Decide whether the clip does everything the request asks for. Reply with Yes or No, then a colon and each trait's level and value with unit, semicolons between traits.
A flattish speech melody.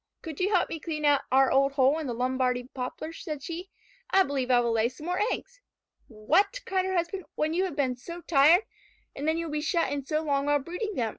No: average, 4.7 semitones